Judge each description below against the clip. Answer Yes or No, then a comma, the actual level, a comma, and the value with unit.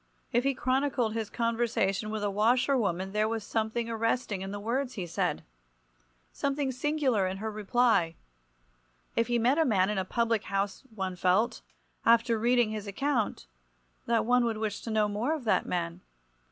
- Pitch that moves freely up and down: No, average, 3.2 semitones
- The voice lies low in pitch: No, high, 225 Hz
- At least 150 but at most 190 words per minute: Yes, average, 175 wpm